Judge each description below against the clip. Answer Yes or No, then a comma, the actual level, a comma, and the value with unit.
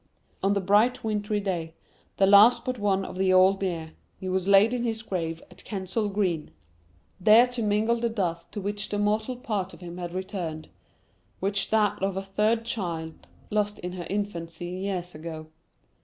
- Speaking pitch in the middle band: No, high, 195 Hz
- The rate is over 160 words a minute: Yes, average, 180 wpm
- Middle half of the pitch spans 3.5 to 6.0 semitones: No, average, 2.9 semitones